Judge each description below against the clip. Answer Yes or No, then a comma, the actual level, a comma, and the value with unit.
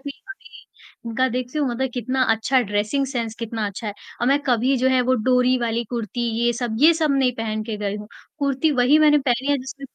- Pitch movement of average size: Yes, average, 3.0 semitones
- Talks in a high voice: Yes, very high, 250 Hz